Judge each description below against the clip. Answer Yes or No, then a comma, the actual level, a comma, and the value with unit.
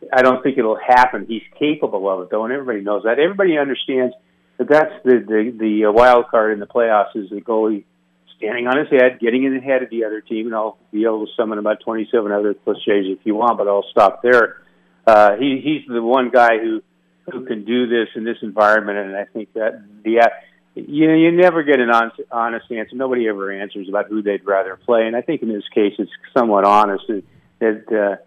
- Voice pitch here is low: Yes, low, 110 Hz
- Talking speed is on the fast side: Yes, fast, 225 wpm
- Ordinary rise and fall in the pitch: Yes, average, 3.0 semitones